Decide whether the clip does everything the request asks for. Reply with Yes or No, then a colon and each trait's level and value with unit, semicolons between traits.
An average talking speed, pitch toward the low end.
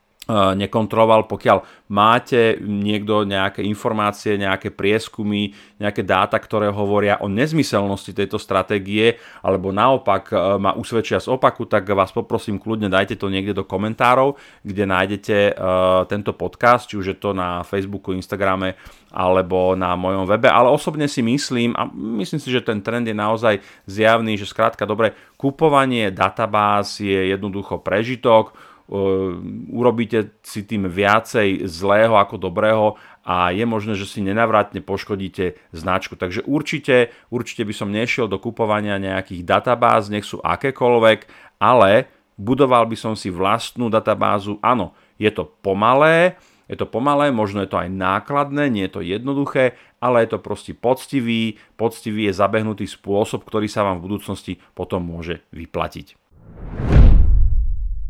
Yes: average, 140 wpm; low, 105 Hz